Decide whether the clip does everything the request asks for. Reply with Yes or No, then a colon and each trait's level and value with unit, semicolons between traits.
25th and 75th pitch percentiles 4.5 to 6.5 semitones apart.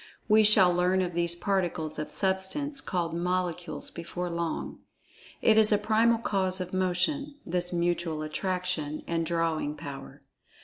No: narrow, 2.4 semitones